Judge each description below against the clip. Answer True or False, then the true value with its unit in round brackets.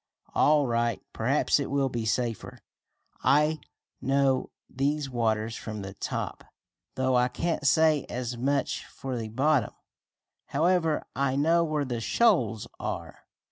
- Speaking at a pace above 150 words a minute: False (135 wpm)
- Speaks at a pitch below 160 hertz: True (135 Hz)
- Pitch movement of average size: True (4.2 semitones)